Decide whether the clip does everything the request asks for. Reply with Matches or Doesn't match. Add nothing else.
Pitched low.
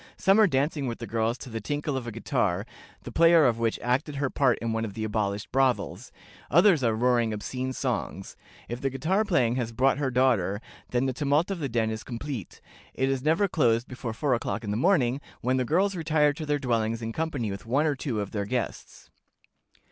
Matches